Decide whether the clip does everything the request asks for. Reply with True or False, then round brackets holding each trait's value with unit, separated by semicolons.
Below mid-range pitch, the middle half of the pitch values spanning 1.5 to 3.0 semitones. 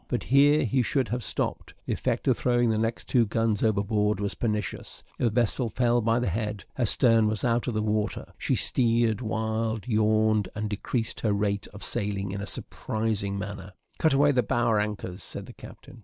True (110 Hz; 2.4 semitones)